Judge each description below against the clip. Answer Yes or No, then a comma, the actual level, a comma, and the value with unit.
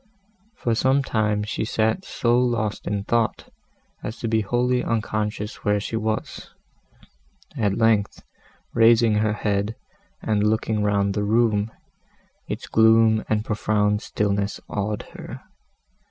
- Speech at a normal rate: No, slow, 125 wpm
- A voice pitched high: No, low, 110 Hz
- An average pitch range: No, narrow, 1.6 semitones